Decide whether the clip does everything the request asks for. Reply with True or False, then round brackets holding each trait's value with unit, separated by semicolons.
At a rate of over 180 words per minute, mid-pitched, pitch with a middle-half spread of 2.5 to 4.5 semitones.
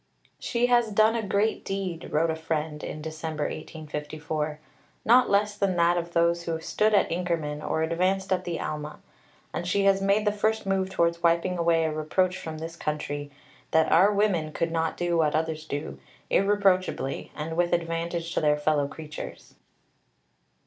False (170 wpm; 170 Hz; 3.6 semitones)